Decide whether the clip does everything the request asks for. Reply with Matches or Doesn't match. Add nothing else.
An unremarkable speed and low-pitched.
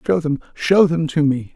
Doesn't match